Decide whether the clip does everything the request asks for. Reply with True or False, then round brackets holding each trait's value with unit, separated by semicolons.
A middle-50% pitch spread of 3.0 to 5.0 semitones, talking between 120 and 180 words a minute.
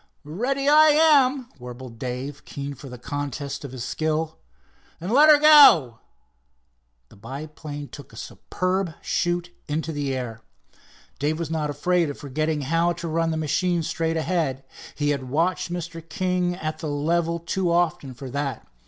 True (3.8 semitones; 160 wpm)